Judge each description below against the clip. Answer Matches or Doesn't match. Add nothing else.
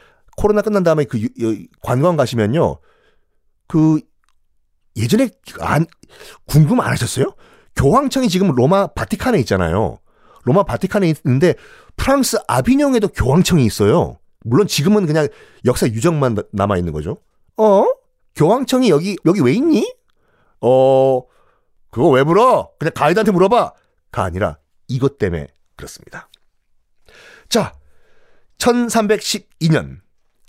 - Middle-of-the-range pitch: Matches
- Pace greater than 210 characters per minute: Matches